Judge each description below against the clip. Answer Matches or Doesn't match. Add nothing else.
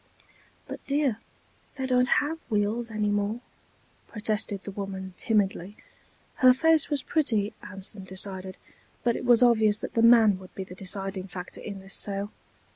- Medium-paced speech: Matches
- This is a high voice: Matches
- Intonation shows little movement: Doesn't match